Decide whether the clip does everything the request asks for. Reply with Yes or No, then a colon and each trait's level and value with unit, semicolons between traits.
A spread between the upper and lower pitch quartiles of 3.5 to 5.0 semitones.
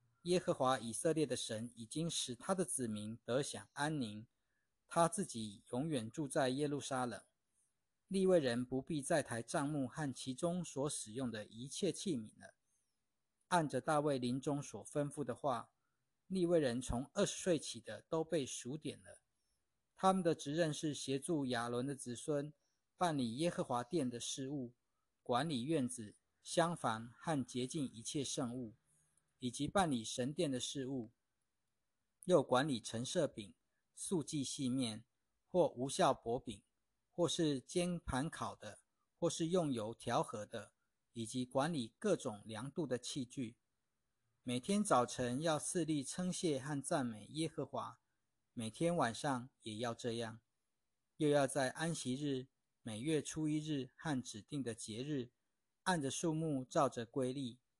Yes: average, 4.7 semitones